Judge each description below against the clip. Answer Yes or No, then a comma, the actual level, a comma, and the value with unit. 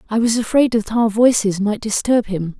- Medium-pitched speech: No, high, 220 Hz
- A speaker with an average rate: No, fast, 210 wpm